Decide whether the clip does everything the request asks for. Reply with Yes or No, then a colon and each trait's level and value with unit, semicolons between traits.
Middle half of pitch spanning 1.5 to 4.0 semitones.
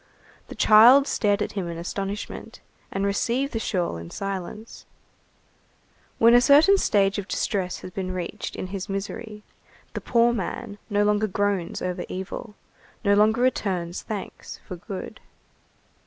Yes: average, 3.1 semitones